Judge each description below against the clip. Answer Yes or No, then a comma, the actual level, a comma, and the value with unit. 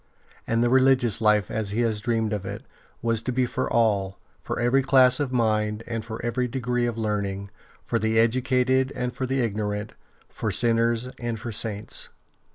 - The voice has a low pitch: Yes, low, 115 Hz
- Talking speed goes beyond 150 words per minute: Yes, average, 180 wpm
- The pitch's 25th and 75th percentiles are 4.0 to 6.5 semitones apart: No, average, 2.7 semitones